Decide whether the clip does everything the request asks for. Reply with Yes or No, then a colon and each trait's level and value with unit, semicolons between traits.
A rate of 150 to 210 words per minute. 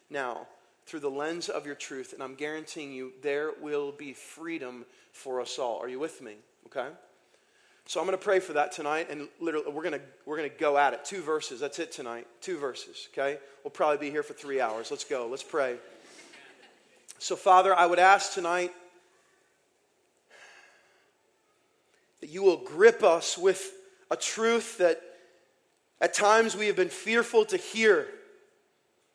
Yes: average, 165 wpm